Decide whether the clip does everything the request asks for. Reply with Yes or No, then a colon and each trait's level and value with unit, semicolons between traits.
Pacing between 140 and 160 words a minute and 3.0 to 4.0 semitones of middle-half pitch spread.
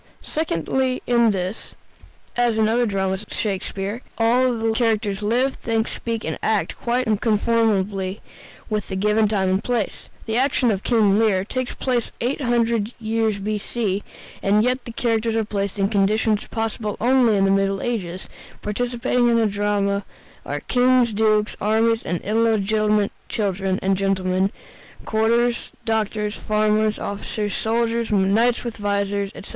No: average, 150 wpm; narrow, 2.6 semitones